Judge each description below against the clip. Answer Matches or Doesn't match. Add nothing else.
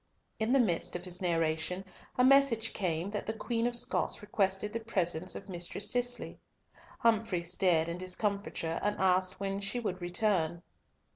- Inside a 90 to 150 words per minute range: Doesn't match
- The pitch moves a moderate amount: Matches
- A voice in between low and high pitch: Doesn't match